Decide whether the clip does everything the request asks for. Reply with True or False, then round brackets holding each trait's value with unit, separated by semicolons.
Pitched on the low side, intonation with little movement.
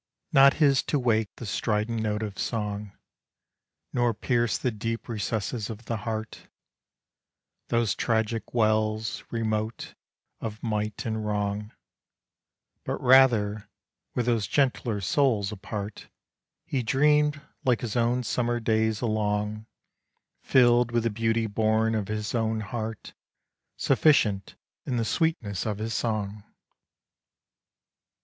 True (110 Hz; 2.1 semitones)